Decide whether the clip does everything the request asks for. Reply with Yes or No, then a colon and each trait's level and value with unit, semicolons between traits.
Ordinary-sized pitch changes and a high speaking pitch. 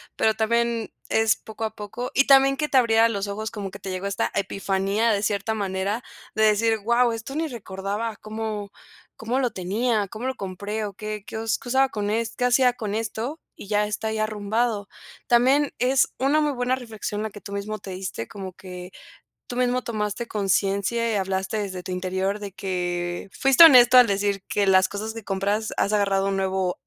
Yes: average, 3.0 semitones; high, 215 Hz